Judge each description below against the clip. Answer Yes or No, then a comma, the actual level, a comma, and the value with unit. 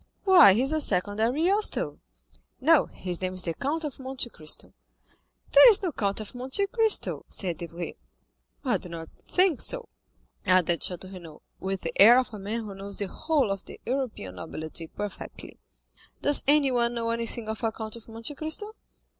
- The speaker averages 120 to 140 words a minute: No, average, 180 wpm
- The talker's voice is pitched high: Yes, high, 230 Hz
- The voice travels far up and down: Yes, wide, 7.3 semitones